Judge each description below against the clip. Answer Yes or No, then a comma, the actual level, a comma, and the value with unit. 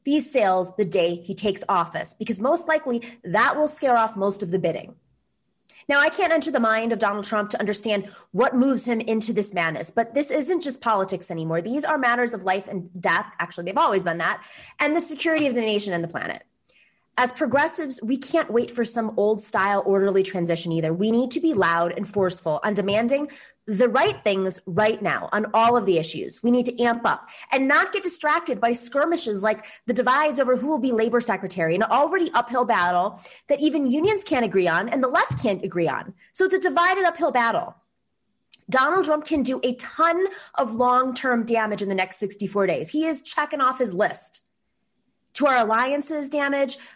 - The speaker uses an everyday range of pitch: No, wide, 6.3 semitones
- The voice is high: Yes, high, 235 Hz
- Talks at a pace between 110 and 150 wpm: No, fast, 205 wpm